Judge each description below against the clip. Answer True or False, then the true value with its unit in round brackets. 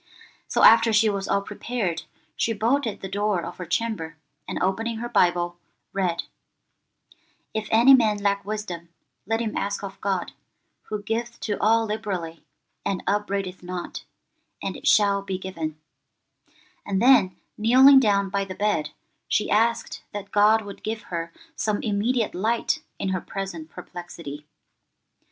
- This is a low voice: False (200 Hz)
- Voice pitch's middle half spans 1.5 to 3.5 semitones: True (3.1 semitones)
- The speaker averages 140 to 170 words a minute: True (145 wpm)